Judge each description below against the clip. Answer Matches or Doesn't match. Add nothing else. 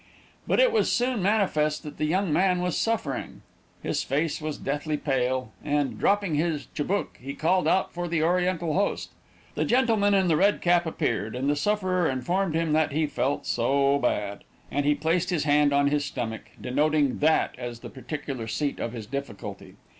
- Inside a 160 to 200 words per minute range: Matches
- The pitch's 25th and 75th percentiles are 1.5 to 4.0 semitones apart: Doesn't match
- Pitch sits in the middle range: Matches